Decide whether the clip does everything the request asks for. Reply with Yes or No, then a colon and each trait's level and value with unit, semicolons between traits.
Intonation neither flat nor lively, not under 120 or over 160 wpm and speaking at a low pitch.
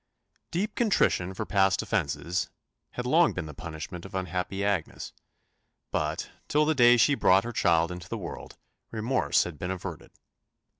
No: wide, 5.7 semitones; average, 155 wpm; very low, 95 Hz